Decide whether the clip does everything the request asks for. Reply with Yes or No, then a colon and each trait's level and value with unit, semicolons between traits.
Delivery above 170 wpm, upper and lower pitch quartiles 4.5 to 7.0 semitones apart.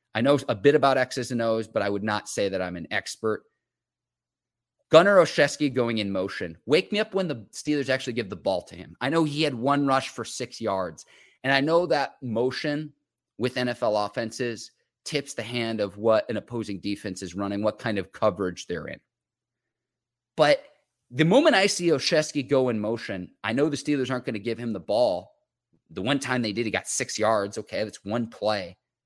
Yes: fast, 205 wpm; average, 4.9 semitones